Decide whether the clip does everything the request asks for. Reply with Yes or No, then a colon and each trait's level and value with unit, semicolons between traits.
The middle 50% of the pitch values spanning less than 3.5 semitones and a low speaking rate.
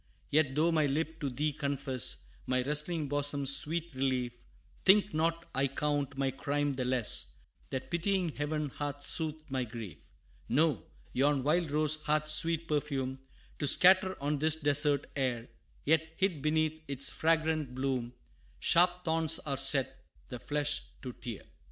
No: average, 2.9 semitones; average, 150 wpm